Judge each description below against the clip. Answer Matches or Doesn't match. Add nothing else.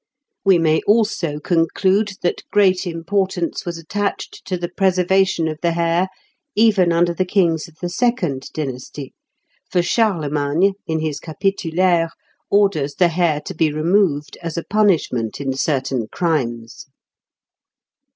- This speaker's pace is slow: Matches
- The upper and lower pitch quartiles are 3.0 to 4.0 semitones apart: Matches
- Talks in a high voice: Doesn't match